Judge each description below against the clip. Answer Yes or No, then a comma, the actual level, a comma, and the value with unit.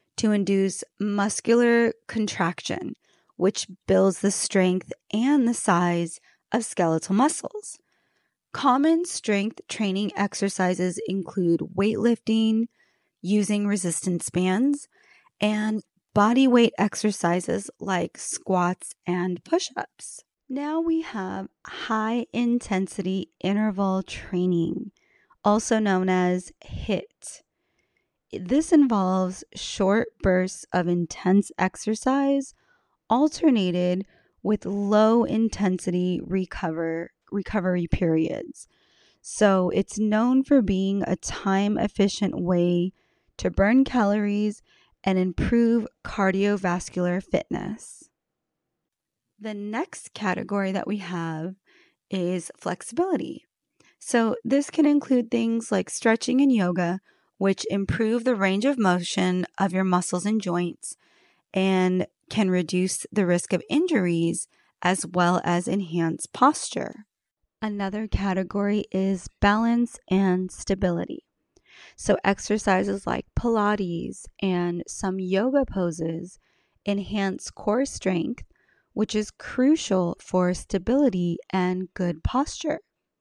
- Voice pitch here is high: Yes, high, 200 Hz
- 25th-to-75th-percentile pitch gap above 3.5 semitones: Yes, average, 3.9 semitones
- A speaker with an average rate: No, slow, 100 wpm